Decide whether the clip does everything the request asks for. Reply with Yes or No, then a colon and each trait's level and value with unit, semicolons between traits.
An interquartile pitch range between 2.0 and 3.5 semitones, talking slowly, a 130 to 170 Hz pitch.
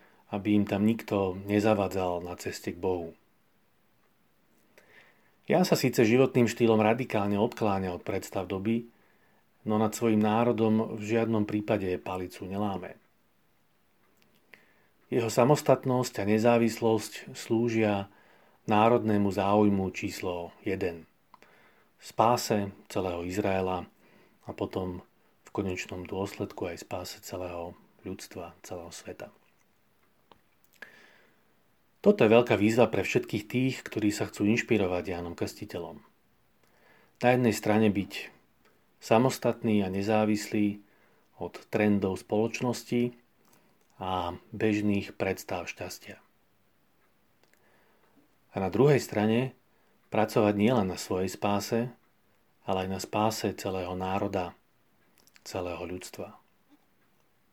No: average, 2.9 semitones; slow, 100 wpm; low, 105 Hz